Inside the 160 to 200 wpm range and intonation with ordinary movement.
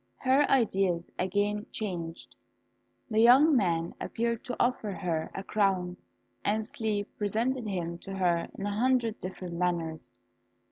No: slow, 135 wpm; average, 4.3 semitones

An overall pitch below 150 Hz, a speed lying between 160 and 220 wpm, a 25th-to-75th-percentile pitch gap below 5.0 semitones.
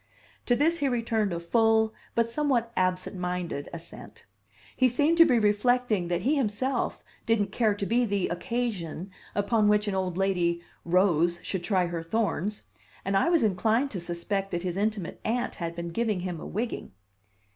No: high, 205 Hz; average, 175 wpm; average, 4.6 semitones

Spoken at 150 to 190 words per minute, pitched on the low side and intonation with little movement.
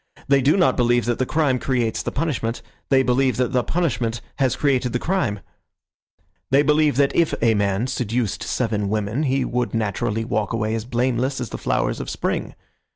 No: average, 185 wpm; low, 125 Hz; average, 3.2 semitones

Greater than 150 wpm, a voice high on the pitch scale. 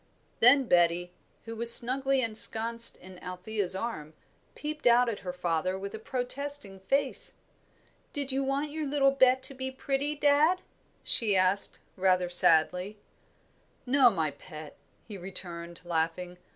No: average, 140 wpm; high, 220 Hz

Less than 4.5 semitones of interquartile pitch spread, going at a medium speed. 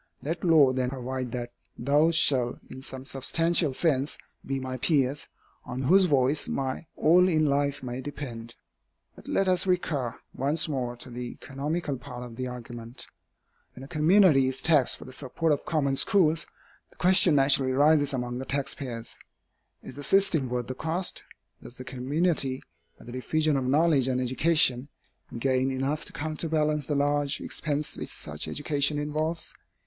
Yes: average, 3.3 semitones; average, 165 wpm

